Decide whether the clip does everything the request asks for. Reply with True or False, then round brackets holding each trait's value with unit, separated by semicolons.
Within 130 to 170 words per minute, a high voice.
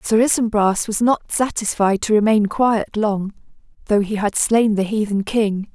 True (165 wpm; 215 Hz)